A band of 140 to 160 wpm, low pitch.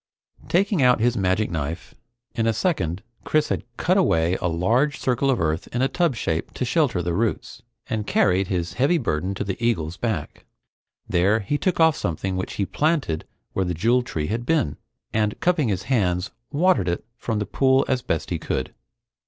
No: average, 190 wpm; low, 110 Hz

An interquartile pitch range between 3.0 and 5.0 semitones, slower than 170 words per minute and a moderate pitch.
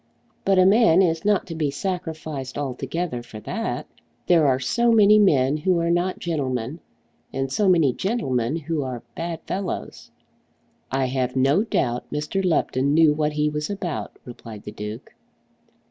No: wide, 5.4 semitones; average, 160 wpm; medium, 150 Hz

